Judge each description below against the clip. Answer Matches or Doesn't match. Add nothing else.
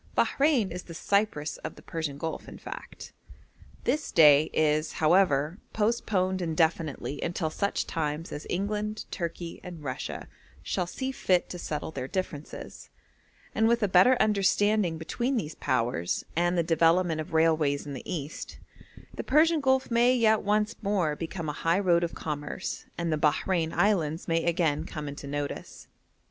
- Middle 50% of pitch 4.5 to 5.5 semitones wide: Matches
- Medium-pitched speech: Matches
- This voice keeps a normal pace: Matches